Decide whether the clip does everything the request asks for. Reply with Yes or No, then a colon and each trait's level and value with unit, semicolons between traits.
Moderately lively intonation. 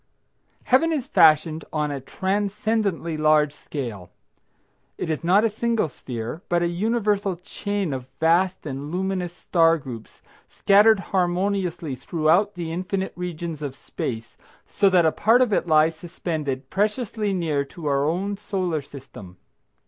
Yes: average, 4.6 semitones